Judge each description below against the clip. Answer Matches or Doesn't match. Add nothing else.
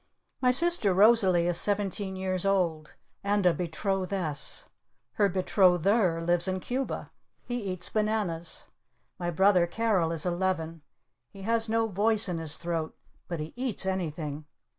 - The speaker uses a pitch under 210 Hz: Matches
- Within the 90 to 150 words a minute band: Matches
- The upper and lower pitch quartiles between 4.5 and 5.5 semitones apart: Doesn't match